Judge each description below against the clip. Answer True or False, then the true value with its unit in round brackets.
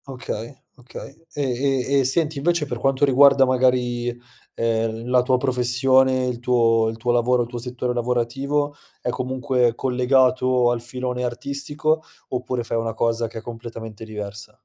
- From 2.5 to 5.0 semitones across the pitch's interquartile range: False (2.0 semitones)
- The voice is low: True (125 Hz)